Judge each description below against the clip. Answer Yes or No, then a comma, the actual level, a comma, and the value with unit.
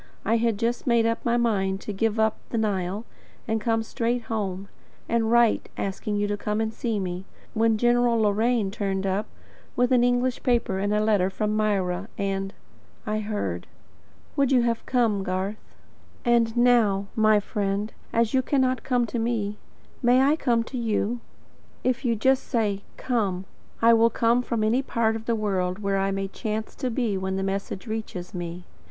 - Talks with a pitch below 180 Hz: No, high, 220 Hz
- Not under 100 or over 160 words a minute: No, average, 185 wpm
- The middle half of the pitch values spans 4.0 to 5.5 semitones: No, average, 3.0 semitones